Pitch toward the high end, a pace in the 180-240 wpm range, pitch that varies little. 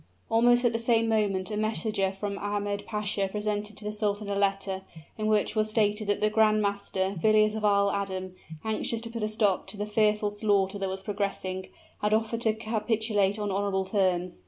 Yes: high, 210 Hz; average, 195 wpm; narrow, 1.5 semitones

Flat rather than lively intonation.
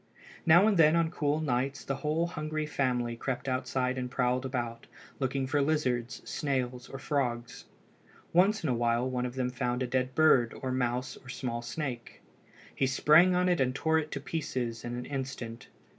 No: average, 3.5 semitones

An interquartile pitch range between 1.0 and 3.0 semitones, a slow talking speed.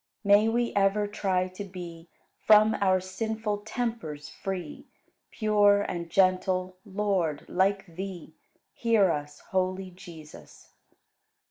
Yes: narrow, 2.5 semitones; slow, 110 wpm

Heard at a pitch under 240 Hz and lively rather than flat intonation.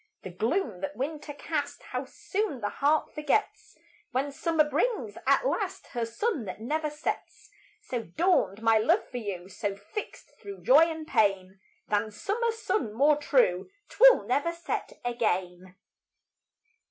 No: very high, 275 Hz; wide, 7.8 semitones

